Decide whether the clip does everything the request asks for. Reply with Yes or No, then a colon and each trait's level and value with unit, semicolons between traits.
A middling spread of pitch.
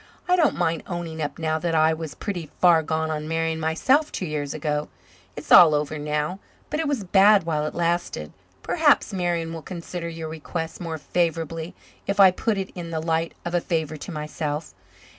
No: narrow, 2.2 semitones